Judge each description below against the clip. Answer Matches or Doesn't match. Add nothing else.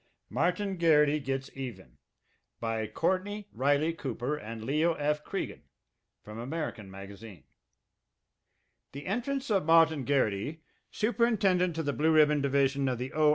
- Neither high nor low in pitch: Matches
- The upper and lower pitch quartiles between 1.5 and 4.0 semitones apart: Doesn't match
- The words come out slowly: Matches